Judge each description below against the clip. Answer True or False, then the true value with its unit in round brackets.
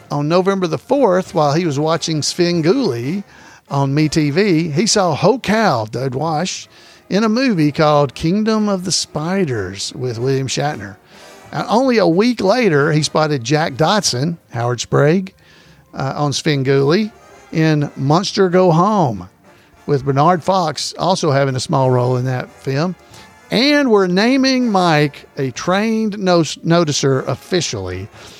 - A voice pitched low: False (155 Hz)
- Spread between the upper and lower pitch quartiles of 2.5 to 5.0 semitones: False (5.4 semitones)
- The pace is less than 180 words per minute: True (140 wpm)